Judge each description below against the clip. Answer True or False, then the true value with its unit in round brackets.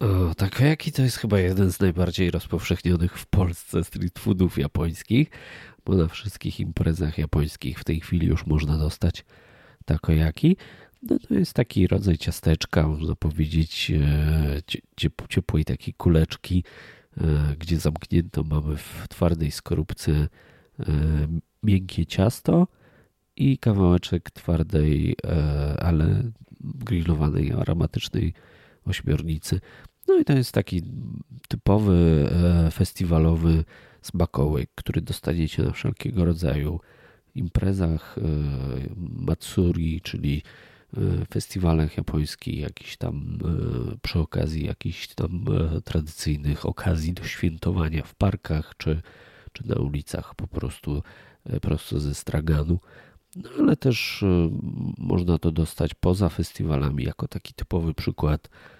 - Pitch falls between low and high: False (85 Hz)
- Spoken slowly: True (105 wpm)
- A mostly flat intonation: False (3.7 semitones)